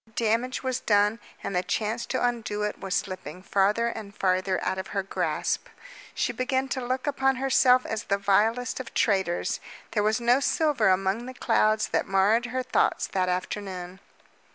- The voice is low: No, high, 215 Hz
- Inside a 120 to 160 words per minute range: No, average, 175 wpm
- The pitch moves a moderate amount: Yes, average, 4.3 semitones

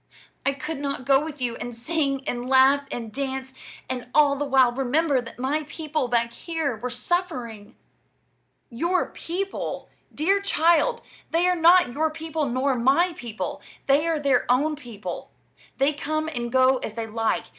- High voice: Yes, very high, 275 Hz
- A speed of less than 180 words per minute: Yes, average, 165 wpm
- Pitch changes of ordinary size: Yes, average, 4.3 semitones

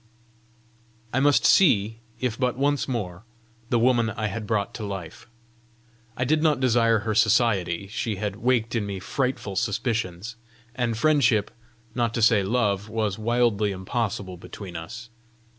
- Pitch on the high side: No, low, 115 Hz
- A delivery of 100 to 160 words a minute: Yes, average, 145 wpm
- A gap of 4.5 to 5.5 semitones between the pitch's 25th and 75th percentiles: No, average, 3.3 semitones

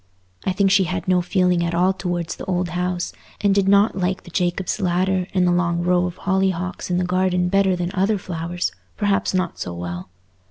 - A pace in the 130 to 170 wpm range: No, average, 200 wpm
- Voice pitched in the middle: Yes, medium, 180 Hz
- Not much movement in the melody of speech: Yes, narrow, 1.3 semitones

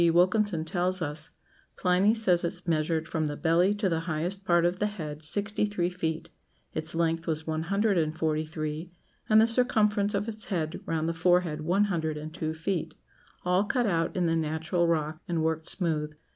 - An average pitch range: Yes, average, 3.3 semitones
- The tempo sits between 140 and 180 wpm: No, average, 190 wpm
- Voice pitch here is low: No, medium, 170 Hz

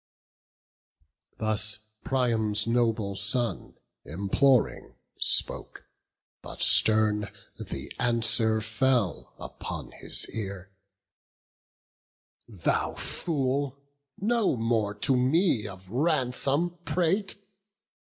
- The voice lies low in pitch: Yes, low, 115 Hz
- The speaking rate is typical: No, slow, 75 wpm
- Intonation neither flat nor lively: Yes, average, 4.2 semitones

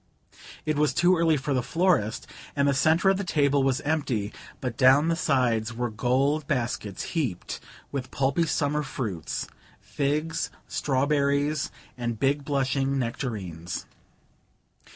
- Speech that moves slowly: Yes, slow, 130 wpm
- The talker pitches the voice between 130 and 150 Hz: Yes, medium, 140 Hz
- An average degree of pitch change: Yes, average, 3.5 semitones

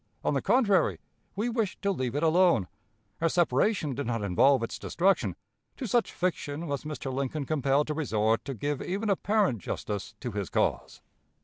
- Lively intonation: Yes, wide, 6.4 semitones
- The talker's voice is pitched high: No, medium, 150 Hz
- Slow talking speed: No, average, 175 wpm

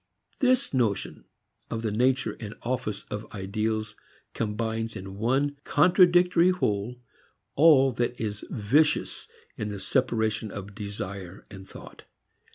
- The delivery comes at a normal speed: No, slow, 120 wpm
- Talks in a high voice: No, low, 110 Hz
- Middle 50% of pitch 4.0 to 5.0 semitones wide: Yes, average, 4.3 semitones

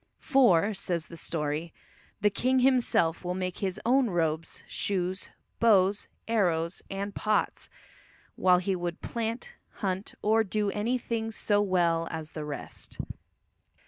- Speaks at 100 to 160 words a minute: Yes, slow, 135 wpm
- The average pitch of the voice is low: No, high, 190 Hz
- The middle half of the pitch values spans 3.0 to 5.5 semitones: Yes, average, 4.4 semitones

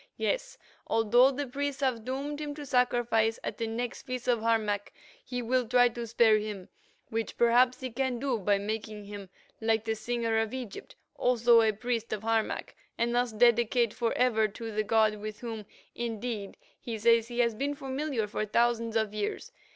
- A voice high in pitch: Yes, high, 230 Hz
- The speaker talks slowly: No, average, 180 wpm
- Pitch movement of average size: No, narrow, 2.3 semitones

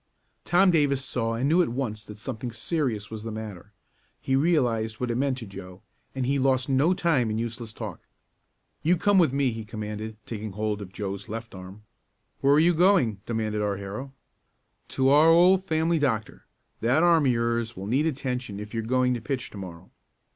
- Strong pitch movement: No, average, 4.7 semitones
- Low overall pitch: Yes, low, 120 Hz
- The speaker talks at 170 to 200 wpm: Yes, average, 195 wpm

